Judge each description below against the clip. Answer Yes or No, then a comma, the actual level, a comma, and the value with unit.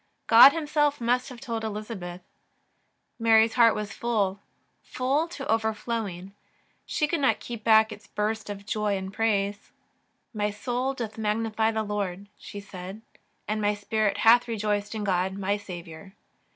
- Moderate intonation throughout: No, narrow, 2.2 semitones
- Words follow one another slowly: No, average, 155 wpm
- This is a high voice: Yes, high, 215 Hz